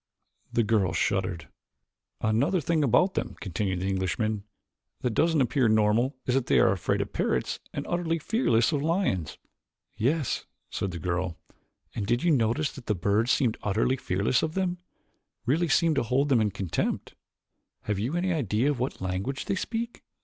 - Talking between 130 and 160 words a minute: No, average, 170 wpm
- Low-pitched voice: Yes, low, 120 Hz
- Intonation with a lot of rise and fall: Yes, wide, 7.2 semitones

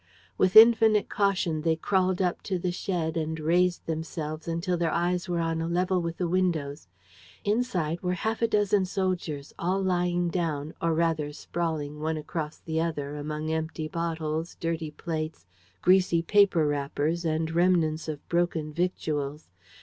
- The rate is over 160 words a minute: No, average, 155 wpm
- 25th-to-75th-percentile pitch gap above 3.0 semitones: No, narrow, 2.5 semitones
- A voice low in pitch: No, medium, 165 Hz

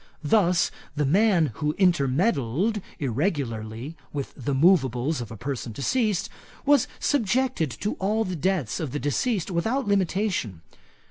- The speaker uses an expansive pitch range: Yes, wide, 7.1 semitones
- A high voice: No, medium, 165 Hz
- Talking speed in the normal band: No, slow, 130 wpm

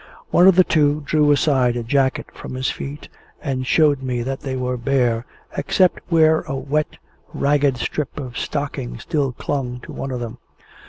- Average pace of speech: Yes, average, 175 wpm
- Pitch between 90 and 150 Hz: Yes, low, 135 Hz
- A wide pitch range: No, average, 2.8 semitones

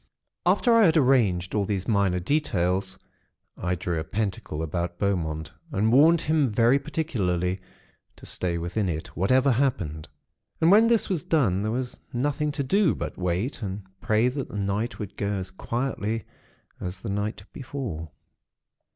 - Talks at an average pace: Yes, average, 160 wpm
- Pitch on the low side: Yes, low, 105 Hz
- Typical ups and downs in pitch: No, wide, 6.9 semitones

